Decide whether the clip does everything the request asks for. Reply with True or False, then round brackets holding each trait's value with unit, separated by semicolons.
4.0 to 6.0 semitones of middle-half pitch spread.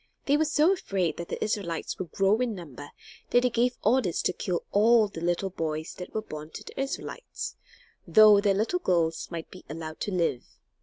True (5.6 semitones)